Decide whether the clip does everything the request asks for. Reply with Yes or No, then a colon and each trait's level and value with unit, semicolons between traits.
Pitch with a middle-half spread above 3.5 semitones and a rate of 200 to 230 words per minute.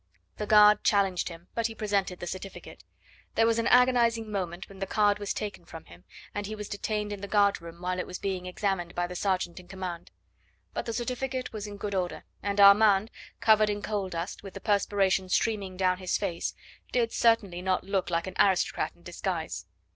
No: narrow, 2.6 semitones; fast, 205 wpm